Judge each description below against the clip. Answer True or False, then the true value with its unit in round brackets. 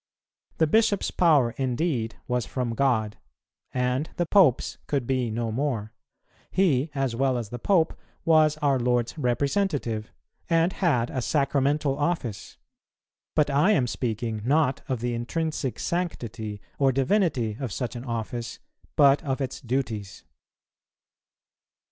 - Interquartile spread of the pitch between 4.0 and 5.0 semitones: True (4.3 semitones)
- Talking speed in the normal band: False (130 wpm)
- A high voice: False (130 Hz)